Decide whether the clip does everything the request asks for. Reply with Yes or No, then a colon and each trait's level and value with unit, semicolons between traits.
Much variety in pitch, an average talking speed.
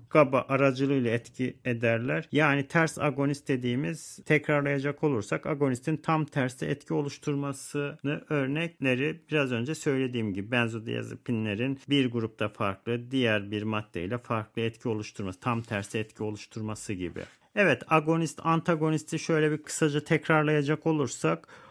No: average, 4.8 semitones; average, 120 wpm